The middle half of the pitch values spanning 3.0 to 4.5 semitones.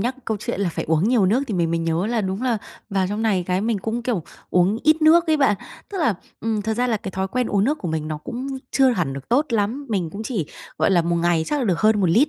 No: average, 5.1 semitones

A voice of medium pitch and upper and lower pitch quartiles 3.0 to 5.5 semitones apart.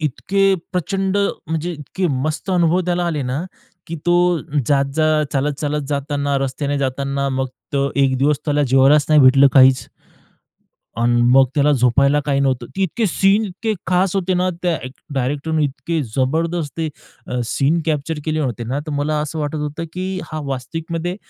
Yes: medium, 150 Hz; average, 3.3 semitones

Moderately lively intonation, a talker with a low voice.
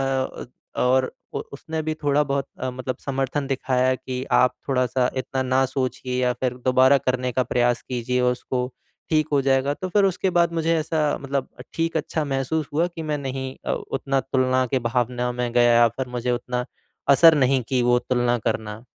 No: narrow, 2.1 semitones; low, 130 Hz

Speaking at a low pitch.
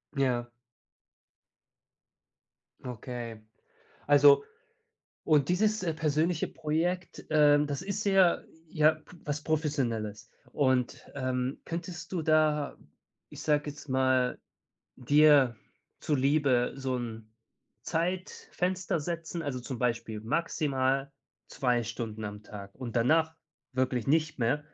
No: medium, 145 Hz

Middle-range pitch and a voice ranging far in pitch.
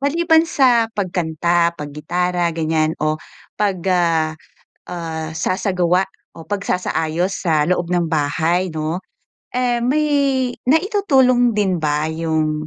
Yes: medium, 180 Hz; wide, 7.0 semitones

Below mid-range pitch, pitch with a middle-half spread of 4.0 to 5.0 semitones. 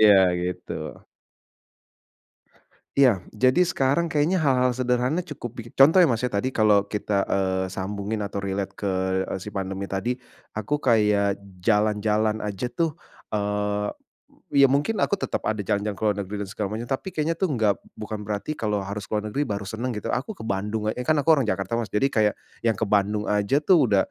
Yes: low, 110 Hz; average, 4.3 semitones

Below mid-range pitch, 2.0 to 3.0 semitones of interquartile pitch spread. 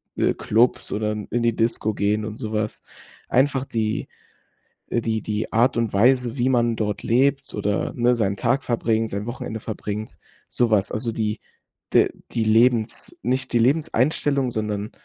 Yes: low, 115 Hz; narrow, 2.5 semitones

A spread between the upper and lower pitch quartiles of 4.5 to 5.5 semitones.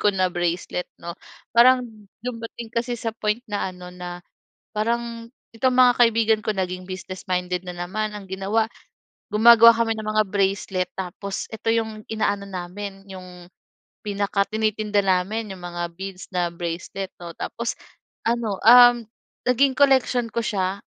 No: average, 3.8 semitones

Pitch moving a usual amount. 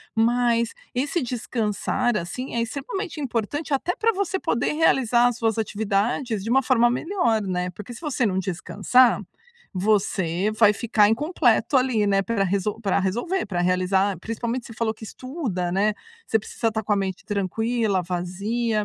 Yes: average, 3.8 semitones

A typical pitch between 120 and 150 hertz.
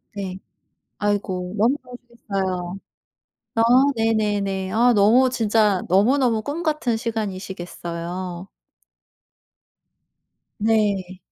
No: high, 205 Hz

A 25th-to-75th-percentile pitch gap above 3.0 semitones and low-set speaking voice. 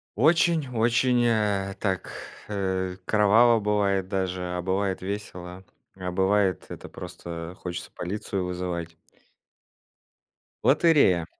No: average, 2.7 semitones; very low, 95 Hz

